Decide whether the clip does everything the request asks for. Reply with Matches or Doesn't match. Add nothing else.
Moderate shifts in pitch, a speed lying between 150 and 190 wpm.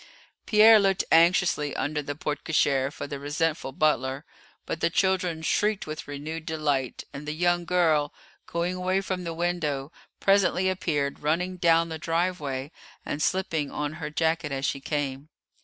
Matches